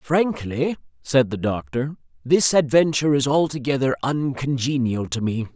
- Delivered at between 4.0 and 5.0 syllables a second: Yes, 4.5 syllables/s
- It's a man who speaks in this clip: Yes, male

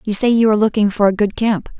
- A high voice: Yes, high, 210 Hz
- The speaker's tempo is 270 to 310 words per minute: Yes, fast, 300 wpm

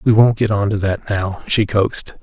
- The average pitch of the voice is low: Yes, low, 105 Hz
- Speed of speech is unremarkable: No, fast, 245 wpm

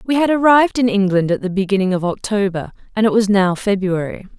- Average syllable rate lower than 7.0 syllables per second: Yes, 6.0 syllables/s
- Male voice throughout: No, female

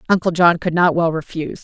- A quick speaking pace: Yes, fast, 220 wpm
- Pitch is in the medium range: Yes, medium, 170 Hz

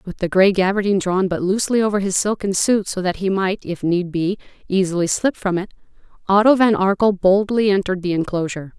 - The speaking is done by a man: No, female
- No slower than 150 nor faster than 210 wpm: Yes, average, 200 wpm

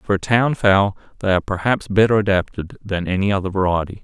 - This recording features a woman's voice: No, male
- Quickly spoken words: No, average, 195 wpm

